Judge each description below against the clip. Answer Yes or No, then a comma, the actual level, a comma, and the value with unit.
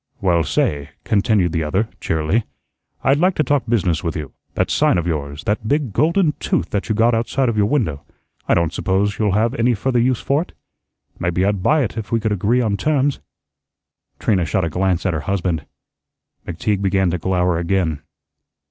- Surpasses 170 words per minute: Yes, average, 190 wpm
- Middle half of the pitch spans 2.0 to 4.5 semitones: No, average, 5.3 semitones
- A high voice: No, low, 100 Hz